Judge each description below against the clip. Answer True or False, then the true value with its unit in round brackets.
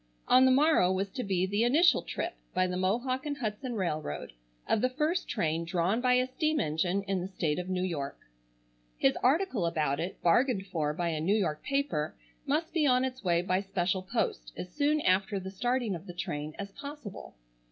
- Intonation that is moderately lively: False (6.6 semitones)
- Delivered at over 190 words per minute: True (200 wpm)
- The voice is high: True (195 Hz)